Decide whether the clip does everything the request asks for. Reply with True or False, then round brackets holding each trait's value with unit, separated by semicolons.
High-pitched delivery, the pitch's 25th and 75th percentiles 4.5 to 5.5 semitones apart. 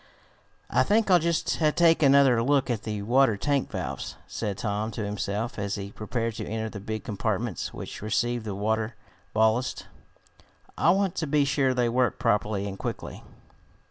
False (115 Hz; 4.8 semitones)